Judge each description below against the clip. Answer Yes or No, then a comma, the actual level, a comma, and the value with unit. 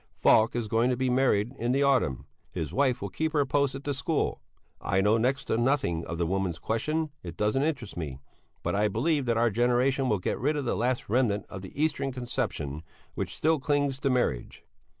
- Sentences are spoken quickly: Yes, fast, 210 wpm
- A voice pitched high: No, low, 125 Hz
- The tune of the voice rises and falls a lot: No, average, 5.0 semitones